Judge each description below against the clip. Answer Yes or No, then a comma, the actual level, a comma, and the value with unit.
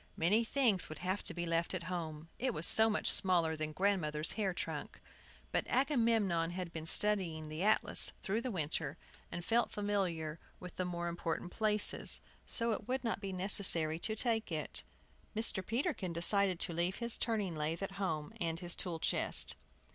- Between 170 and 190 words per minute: Yes, average, 185 wpm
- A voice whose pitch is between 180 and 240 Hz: Yes, medium, 185 Hz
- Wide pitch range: No, average, 4.4 semitones